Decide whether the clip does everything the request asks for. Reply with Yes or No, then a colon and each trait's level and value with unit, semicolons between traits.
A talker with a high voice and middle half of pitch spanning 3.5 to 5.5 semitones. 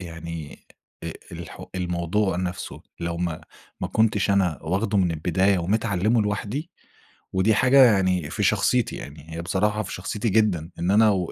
No: very low, 95 Hz; average, 3.8 semitones